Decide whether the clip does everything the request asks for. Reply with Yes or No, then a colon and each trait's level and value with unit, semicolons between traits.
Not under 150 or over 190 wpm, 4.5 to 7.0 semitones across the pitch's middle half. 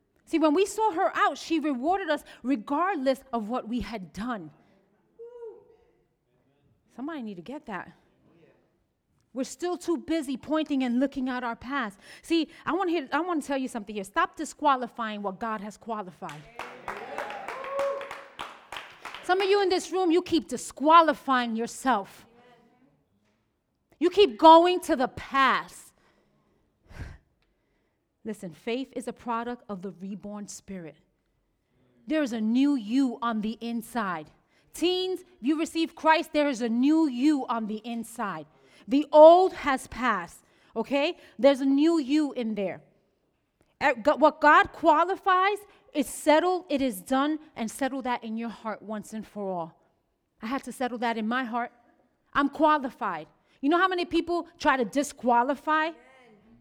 No: average, 140 wpm; wide, 5.6 semitones